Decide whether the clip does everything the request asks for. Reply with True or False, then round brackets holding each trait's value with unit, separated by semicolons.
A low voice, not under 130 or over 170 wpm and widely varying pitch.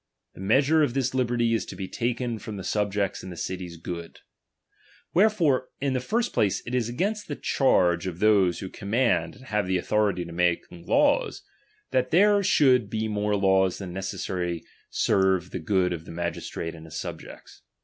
False (105 Hz; 200 wpm; 6.0 semitones)